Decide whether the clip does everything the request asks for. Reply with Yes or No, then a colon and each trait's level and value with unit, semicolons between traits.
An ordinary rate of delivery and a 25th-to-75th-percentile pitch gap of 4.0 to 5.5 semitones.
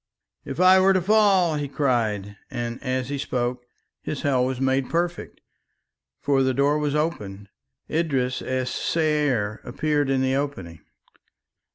No: average, 145 wpm; average, 3.4 semitones